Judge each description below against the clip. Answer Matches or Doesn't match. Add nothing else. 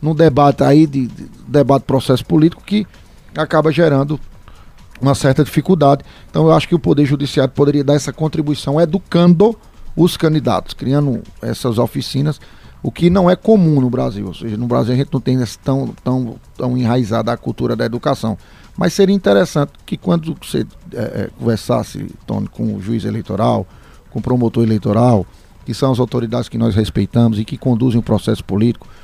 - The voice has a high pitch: Doesn't match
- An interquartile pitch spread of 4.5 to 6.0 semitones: Matches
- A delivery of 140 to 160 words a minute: Doesn't match